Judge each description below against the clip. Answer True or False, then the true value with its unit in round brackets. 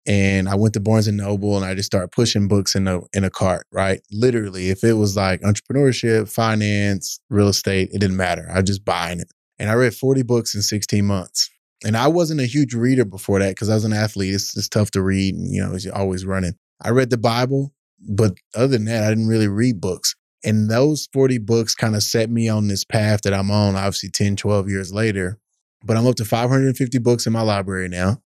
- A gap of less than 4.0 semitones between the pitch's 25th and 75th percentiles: True (3.0 semitones)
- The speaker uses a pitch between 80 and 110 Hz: True (105 Hz)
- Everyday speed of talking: False (235 wpm)